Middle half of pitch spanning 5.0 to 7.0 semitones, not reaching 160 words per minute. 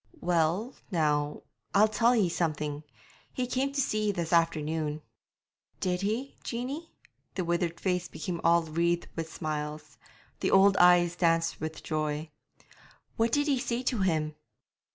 Yes: average, 5.3 semitones; average, 145 wpm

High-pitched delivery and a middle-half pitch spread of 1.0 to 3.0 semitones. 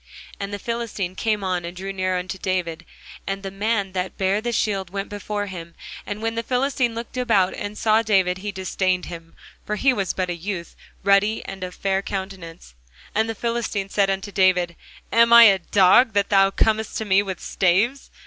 Yes: high, 195 Hz; average, 2.7 semitones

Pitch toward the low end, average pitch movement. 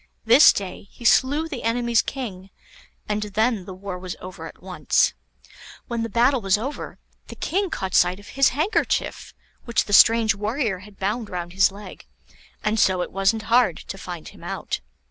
No: high, 210 Hz; average, 3.9 semitones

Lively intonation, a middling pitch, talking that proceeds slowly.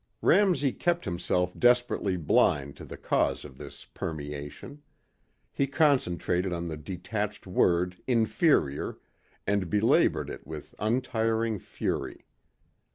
No: wide, 6.2 semitones; low, 100 Hz; slow, 110 wpm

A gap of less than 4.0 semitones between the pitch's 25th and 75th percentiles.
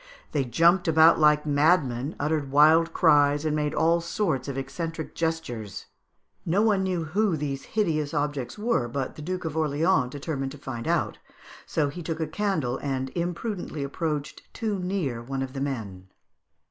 Yes: average, 3.6 semitones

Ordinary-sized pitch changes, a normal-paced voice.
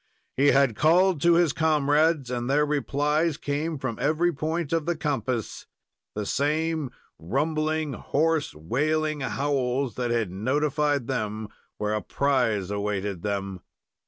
No: average, 4.8 semitones; slow, 130 wpm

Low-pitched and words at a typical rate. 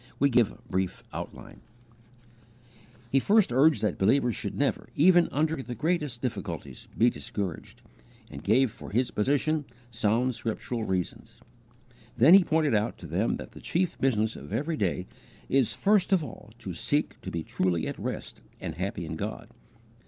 Yes: low, 120 Hz; average, 165 wpm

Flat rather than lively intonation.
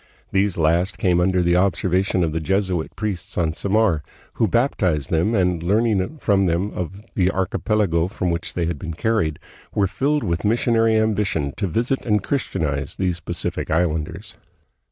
No: average, 3.8 semitones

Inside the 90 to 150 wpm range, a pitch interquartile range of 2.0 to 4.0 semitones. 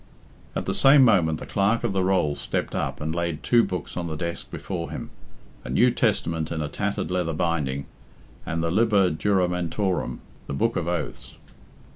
No: average, 180 wpm; average, 3.5 semitones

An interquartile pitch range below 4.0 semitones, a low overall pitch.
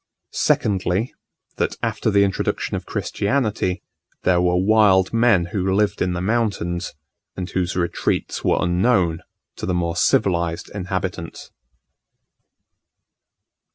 Yes: narrow, 2.6 semitones; very low, 95 Hz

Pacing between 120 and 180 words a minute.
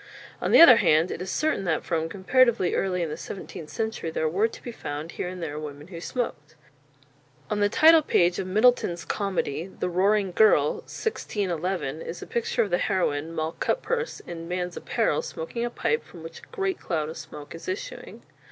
No: average, 195 wpm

